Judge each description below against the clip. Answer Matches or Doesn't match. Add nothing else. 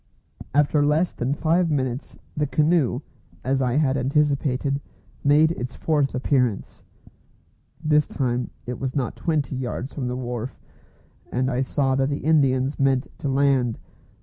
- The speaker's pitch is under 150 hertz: Matches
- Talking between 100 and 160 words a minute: Matches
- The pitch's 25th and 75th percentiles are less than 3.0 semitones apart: Matches